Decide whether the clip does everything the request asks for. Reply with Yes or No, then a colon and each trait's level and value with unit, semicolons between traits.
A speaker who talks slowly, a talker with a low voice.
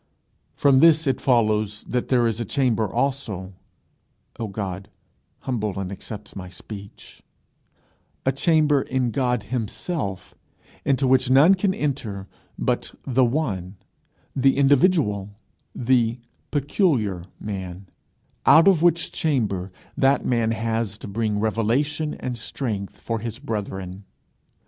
Yes: slow, 120 wpm; low, 115 Hz